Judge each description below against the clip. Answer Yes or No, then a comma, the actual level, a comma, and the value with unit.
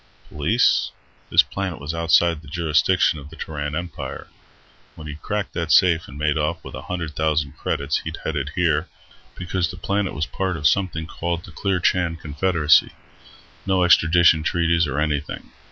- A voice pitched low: Yes, very low, 80 Hz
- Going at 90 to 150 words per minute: No, average, 165 wpm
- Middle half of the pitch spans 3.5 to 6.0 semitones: No, average, 2.8 semitones